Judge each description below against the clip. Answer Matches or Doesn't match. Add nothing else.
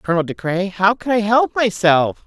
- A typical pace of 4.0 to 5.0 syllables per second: Matches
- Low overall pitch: Doesn't match